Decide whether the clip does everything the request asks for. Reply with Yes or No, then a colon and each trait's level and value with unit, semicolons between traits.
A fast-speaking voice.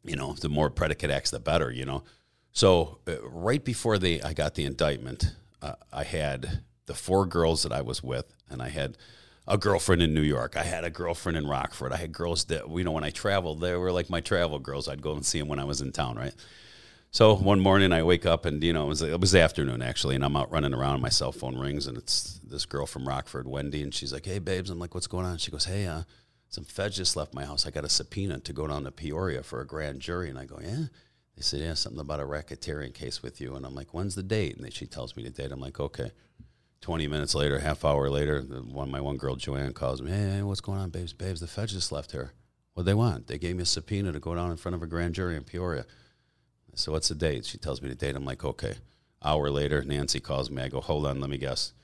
Yes: fast, 270 wpm